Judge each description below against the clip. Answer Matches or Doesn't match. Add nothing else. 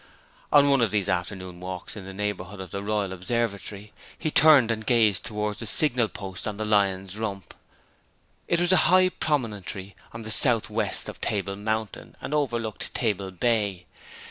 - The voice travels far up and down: Doesn't match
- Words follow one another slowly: Doesn't match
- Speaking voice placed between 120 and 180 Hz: Doesn't match